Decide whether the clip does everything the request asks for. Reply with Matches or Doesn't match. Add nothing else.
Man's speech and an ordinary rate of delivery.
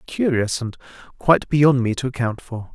Matches